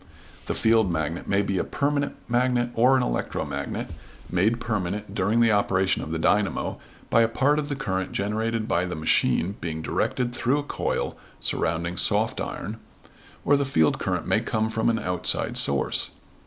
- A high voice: No, low, 110 Hz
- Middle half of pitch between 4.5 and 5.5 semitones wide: Yes, average, 5.0 semitones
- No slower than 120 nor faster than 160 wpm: No, average, 170 wpm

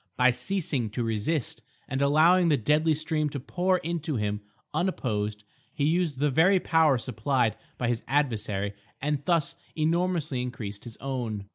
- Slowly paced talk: No, average, 150 wpm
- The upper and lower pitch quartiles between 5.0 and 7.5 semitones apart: Yes, wide, 5.6 semitones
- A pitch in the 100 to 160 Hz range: Yes, medium, 140 Hz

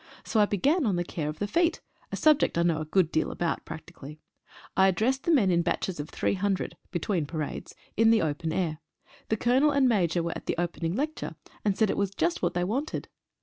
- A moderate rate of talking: No, fast, 220 wpm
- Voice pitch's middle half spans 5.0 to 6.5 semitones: Yes, average, 5.3 semitones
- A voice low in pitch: No, medium, 185 Hz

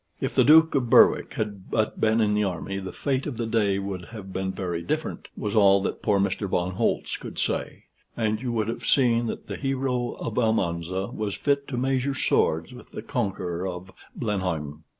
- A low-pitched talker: Yes, low, 105 Hz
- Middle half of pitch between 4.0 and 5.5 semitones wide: Yes, average, 4.4 semitones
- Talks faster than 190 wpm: Yes, average, 200 wpm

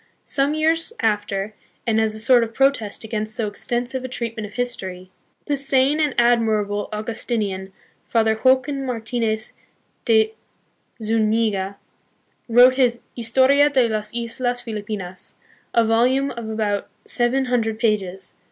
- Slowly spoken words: Yes, slow, 130 wpm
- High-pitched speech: Yes, high, 230 Hz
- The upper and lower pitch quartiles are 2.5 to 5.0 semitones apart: Yes, average, 3.0 semitones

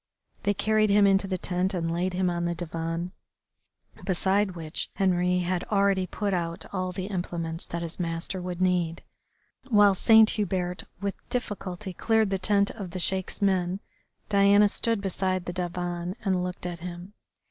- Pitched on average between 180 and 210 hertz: Yes, medium, 185 Hz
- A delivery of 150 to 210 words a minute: Yes, average, 165 wpm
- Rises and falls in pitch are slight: Yes, narrow, 2.1 semitones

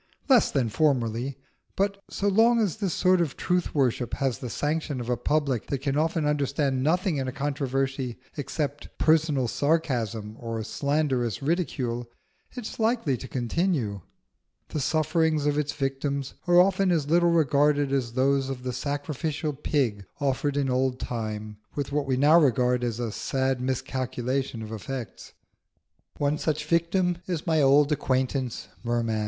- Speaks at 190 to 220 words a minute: No, average, 155 wpm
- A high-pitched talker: No, medium, 140 Hz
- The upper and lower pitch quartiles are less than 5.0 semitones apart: Yes, average, 3.7 semitones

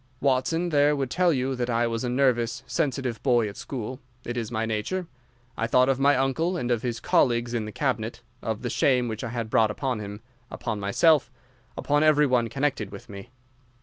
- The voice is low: Yes, low, 125 Hz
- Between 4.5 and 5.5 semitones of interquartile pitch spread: No, average, 3.1 semitones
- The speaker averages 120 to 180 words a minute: No, fast, 205 wpm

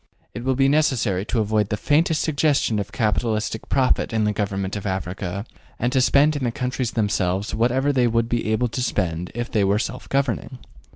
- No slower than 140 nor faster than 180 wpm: No, average, 195 wpm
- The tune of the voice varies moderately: Yes, average, 4.0 semitones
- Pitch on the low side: Yes, low, 115 Hz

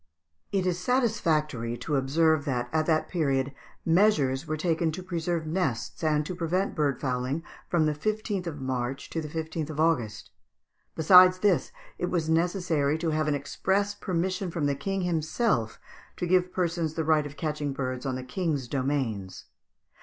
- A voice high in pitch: No, medium, 155 Hz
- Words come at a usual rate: Yes, average, 170 wpm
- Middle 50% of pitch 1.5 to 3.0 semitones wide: No, average, 4.2 semitones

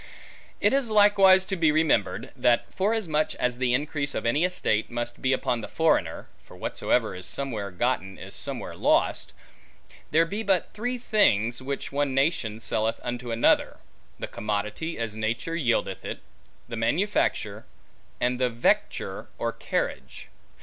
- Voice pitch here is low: Yes, low, 130 Hz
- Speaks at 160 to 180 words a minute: No, average, 150 wpm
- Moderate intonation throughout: No, wide, 6.6 semitones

